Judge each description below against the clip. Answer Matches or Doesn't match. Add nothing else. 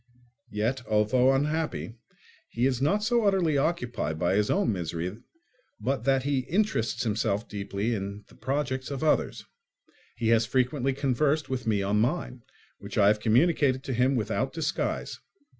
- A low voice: Matches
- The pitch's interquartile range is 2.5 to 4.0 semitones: Doesn't match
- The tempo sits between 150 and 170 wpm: Matches